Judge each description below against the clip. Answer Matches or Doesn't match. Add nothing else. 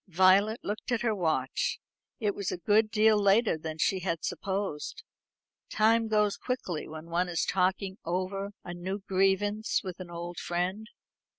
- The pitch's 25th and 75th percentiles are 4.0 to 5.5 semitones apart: Doesn't match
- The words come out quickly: Doesn't match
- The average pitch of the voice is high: Matches